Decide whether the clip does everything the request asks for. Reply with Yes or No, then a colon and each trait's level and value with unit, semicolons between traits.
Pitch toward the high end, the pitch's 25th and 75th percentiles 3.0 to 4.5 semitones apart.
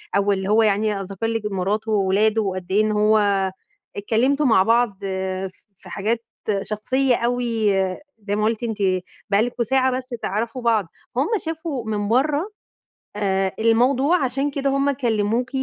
Yes: high, 220 Hz; average, 3.7 semitones